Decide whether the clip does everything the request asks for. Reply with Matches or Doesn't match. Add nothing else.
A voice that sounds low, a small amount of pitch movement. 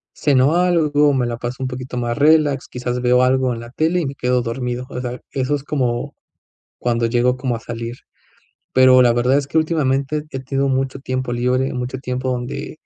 Matches